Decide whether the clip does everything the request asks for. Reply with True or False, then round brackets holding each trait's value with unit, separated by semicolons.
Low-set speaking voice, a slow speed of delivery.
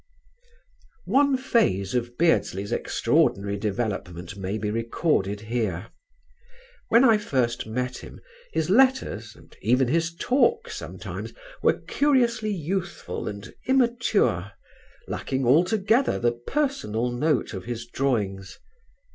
True (125 Hz; 110 wpm)